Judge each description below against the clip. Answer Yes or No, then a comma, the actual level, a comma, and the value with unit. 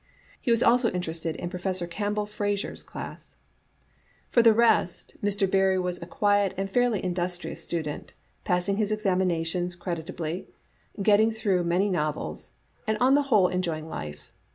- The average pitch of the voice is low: No, medium, 185 Hz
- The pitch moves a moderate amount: Yes, average, 3.2 semitones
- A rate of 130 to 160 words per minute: Yes, average, 155 wpm